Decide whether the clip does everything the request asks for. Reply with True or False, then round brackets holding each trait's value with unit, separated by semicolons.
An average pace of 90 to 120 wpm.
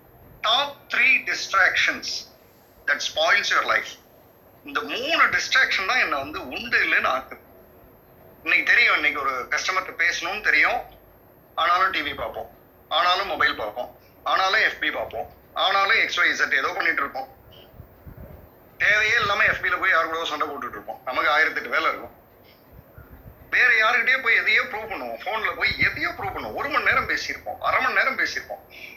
False (130 wpm)